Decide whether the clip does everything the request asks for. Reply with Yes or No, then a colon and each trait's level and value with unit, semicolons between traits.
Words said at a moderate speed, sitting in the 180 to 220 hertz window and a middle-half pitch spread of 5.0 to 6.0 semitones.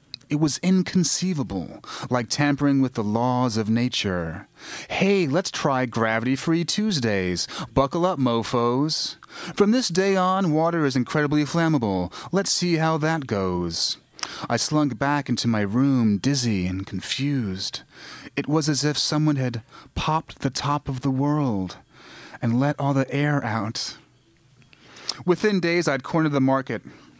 No: average, 145 wpm; medium, 140 Hz; wide, 5.4 semitones